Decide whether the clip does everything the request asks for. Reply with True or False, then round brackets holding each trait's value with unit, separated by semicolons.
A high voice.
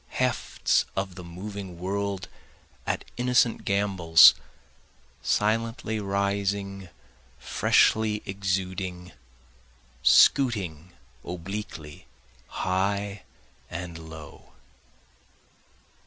False (95 Hz)